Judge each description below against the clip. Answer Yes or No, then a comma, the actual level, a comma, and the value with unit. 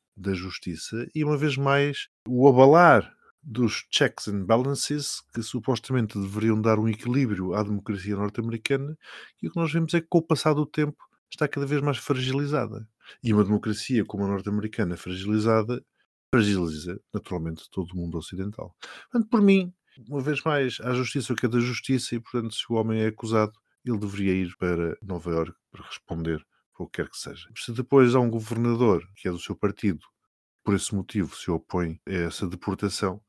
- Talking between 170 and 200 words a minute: Yes, average, 180 wpm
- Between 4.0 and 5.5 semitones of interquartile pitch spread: Yes, average, 5.1 semitones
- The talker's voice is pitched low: Yes, low, 110 Hz